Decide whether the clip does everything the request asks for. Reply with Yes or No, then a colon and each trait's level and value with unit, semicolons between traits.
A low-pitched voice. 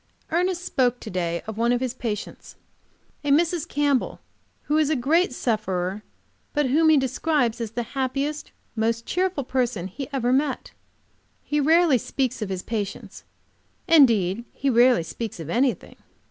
No: very high, 255 Hz